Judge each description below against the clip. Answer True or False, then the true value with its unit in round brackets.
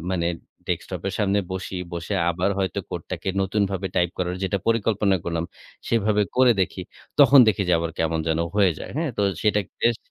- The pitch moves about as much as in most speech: True (3.1 semitones)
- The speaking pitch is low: True (95 Hz)